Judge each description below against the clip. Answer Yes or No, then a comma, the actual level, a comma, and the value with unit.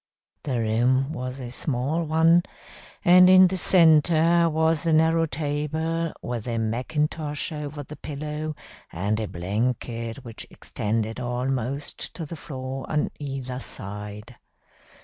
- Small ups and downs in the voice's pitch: No, average, 4.7 semitones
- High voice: No, medium, 140 Hz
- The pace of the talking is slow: Yes, slow, 130 wpm